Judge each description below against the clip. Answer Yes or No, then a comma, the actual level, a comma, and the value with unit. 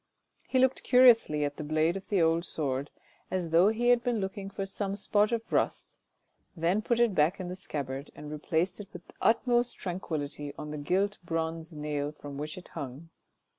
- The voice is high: No, medium, 170 Hz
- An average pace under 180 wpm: No, average, 195 wpm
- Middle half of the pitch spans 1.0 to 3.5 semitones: No, average, 5.3 semitones